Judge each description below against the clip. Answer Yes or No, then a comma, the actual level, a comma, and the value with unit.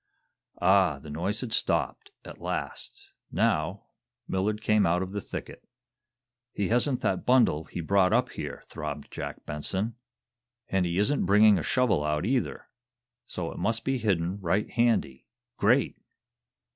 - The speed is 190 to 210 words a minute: No, average, 145 wpm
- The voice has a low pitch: Yes, low, 100 Hz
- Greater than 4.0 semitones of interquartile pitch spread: Yes, average, 4.5 semitones